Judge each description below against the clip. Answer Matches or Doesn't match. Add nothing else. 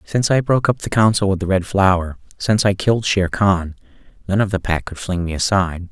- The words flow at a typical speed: Doesn't match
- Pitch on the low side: Matches